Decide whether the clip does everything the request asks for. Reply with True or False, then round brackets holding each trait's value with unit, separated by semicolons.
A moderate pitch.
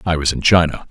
False (80 Hz)